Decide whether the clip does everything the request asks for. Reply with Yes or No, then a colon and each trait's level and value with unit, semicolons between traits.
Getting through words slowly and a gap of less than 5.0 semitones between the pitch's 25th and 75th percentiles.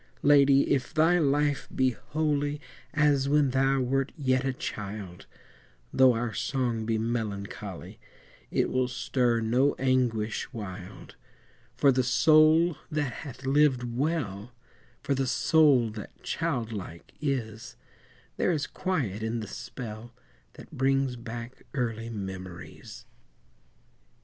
Yes: slow, 120 wpm; average, 3.9 semitones